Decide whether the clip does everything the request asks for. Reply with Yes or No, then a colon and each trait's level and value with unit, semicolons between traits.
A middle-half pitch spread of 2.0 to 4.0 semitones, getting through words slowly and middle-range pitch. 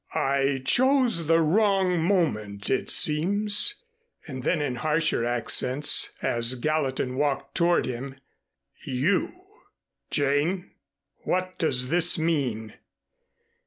No: wide, 5.4 semitones; slow, 100 wpm; medium, 150 Hz